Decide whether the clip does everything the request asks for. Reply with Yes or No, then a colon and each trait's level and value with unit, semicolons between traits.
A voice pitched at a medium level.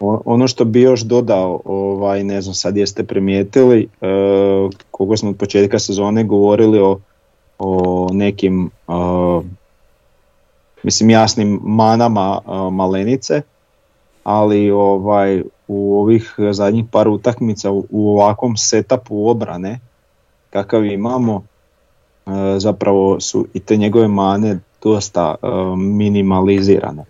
No: low, 100 Hz